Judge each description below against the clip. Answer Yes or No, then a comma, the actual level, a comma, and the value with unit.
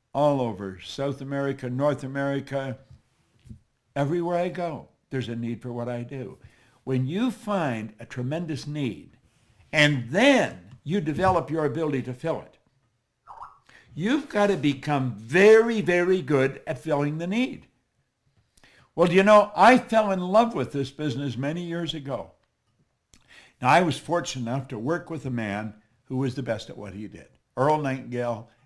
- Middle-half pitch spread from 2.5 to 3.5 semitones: No, average, 5.3 semitones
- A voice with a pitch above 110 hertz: Yes, medium, 140 Hz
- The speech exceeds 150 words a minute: Yes, average, 160 wpm